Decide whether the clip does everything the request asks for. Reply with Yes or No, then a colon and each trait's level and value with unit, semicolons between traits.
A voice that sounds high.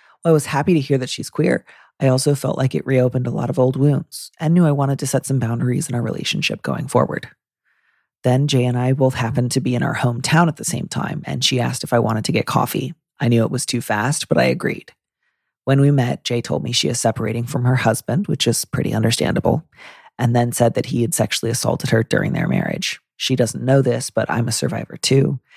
No: low, 130 Hz